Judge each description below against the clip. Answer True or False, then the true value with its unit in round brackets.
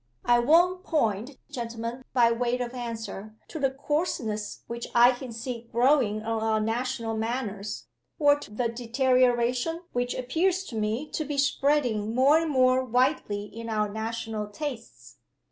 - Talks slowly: False (150 wpm)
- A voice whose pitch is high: True (240 Hz)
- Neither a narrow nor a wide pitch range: True (3.0 semitones)